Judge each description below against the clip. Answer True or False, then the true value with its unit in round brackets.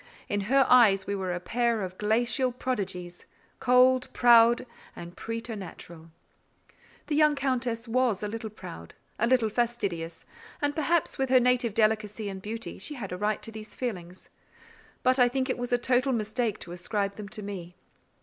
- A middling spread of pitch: True (3.9 semitones)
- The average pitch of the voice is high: True (225 Hz)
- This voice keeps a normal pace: True (170 wpm)